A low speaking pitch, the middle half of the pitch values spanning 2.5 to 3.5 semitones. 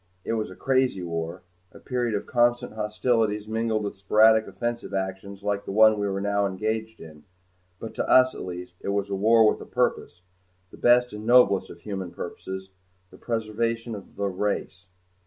Yes: low, 105 Hz; average, 2.9 semitones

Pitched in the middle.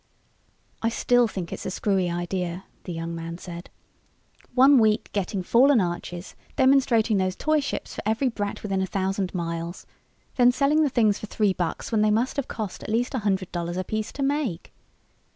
No: high, 205 Hz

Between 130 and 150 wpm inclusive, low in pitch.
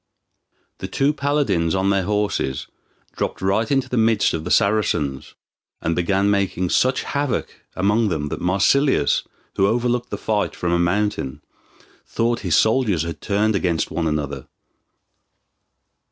Yes: average, 140 wpm; low, 100 Hz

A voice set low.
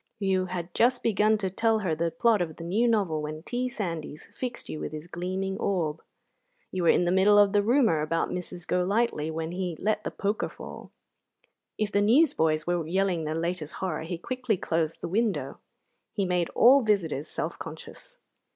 No: medium, 185 Hz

